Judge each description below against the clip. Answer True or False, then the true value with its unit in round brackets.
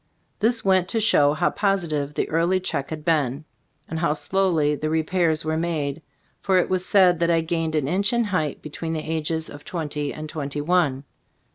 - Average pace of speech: True (190 wpm)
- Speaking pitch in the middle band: True (160 Hz)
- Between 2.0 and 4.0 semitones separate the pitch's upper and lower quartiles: True (3.3 semitones)